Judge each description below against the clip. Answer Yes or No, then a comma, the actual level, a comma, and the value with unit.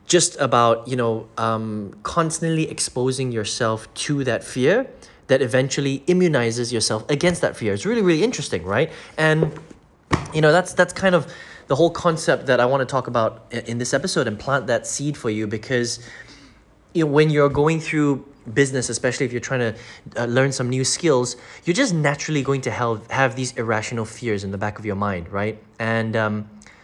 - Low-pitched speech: Yes, low, 125 Hz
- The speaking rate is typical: Yes, average, 185 wpm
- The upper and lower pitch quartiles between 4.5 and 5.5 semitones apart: Yes, average, 4.9 semitones